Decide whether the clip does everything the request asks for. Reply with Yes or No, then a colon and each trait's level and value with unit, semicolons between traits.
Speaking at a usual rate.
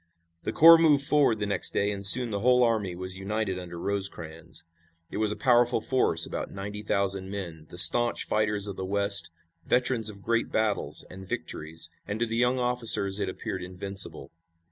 Yes: average, 185 wpm